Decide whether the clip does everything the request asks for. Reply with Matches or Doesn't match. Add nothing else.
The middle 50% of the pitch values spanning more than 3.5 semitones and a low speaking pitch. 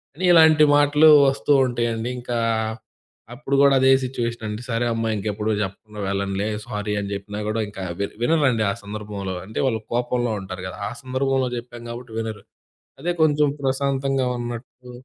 Matches